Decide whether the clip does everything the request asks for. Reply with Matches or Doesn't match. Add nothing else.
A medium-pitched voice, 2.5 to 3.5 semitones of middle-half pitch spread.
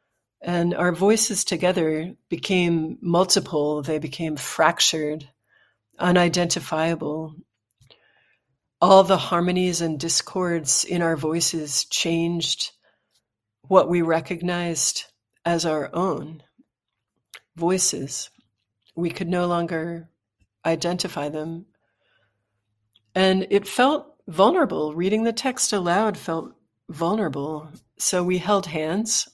Matches